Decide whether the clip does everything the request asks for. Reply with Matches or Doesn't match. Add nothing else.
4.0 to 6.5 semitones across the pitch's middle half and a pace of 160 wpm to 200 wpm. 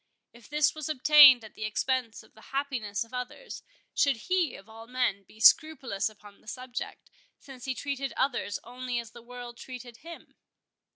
Doesn't match